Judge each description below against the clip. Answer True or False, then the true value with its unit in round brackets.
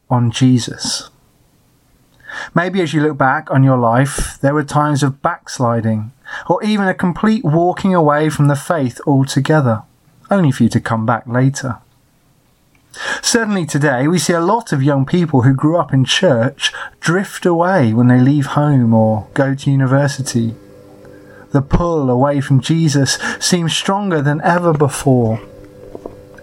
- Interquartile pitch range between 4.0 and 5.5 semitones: True (4.8 semitones)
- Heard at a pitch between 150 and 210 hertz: False (140 Hz)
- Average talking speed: True (150 wpm)